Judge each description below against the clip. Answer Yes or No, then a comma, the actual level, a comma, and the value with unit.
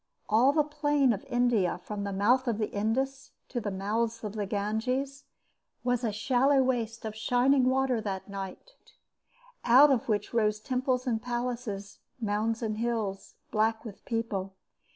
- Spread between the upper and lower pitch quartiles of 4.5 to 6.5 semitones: No, average, 3.2 semitones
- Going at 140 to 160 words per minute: Yes, average, 155 wpm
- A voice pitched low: No, high, 230 Hz